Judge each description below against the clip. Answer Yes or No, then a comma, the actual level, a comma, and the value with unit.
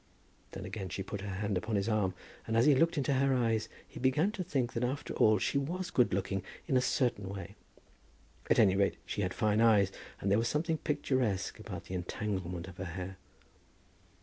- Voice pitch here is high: No, low, 110 Hz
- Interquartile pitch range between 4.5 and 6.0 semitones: Yes, average, 5.3 semitones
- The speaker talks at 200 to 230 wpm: Yes, fast, 205 wpm